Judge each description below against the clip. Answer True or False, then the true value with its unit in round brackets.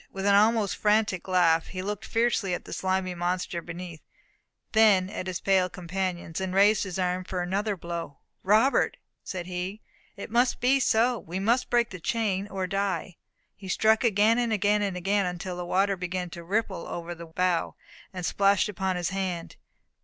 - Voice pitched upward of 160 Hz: True (190 Hz)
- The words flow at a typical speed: True (175 wpm)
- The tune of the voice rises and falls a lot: False (2.6 semitones)